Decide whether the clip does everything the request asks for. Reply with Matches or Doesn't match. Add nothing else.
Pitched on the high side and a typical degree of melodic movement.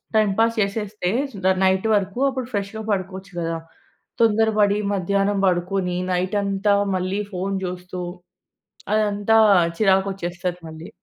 Doesn't match